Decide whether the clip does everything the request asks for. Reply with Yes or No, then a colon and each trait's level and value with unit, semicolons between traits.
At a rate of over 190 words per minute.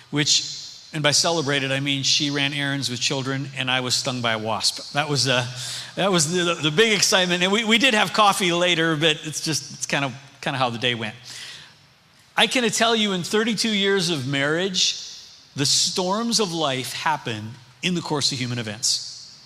Yes: fast, 205 wpm